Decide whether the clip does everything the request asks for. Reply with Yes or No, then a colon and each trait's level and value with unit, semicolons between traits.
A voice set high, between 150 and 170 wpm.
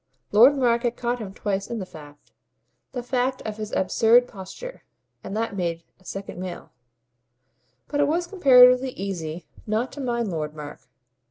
Yes: high, 225 Hz; average, 165 wpm